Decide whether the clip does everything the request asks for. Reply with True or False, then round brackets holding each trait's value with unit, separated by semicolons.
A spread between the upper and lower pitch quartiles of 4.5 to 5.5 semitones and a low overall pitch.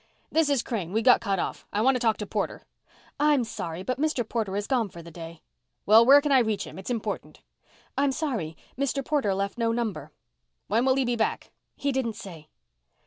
False (5.0 semitones; 230 Hz)